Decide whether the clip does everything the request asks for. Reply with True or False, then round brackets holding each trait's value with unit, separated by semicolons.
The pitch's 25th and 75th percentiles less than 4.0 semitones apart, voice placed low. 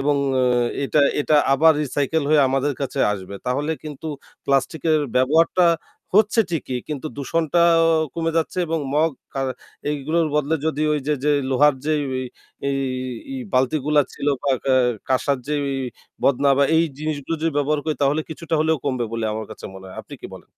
False (2.8 semitones; 150 Hz)